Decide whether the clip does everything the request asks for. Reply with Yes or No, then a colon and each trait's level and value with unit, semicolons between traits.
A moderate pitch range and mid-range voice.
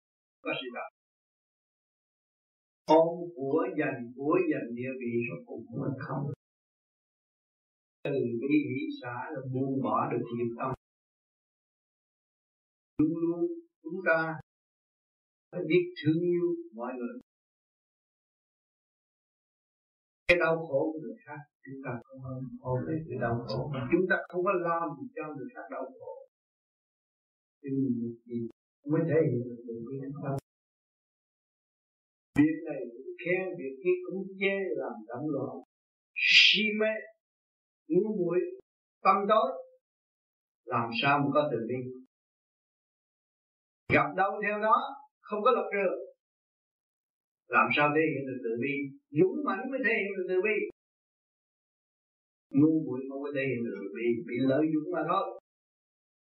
No: wide, 7.3 semitones; medium, 155 Hz